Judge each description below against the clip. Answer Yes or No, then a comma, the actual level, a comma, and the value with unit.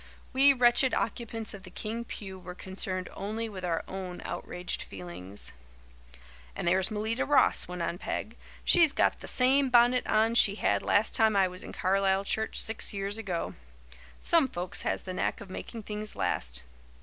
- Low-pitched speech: No, high, 200 Hz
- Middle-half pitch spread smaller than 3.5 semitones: No, average, 3.9 semitones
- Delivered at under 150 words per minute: No, average, 175 wpm